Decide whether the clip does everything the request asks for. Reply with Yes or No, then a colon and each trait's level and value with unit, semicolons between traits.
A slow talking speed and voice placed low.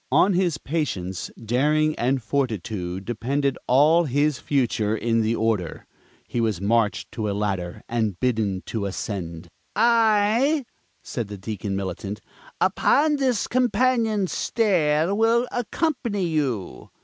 Yes: slow, 125 wpm; low, 130 Hz